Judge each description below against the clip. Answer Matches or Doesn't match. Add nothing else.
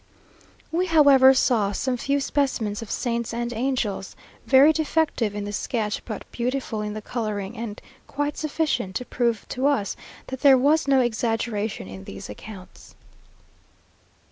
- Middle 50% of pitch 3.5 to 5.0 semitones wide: Matches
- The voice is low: Doesn't match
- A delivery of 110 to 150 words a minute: Matches